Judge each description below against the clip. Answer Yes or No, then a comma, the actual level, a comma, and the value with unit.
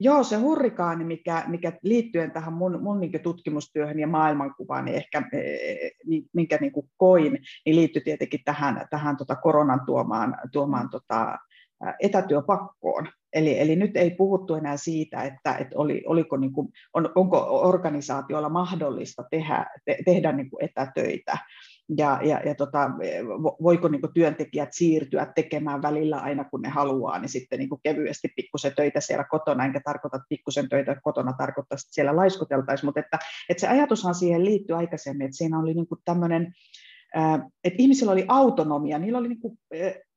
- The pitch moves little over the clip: No, average, 3.7 semitones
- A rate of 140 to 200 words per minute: Yes, average, 150 wpm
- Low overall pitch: No, medium, 160 Hz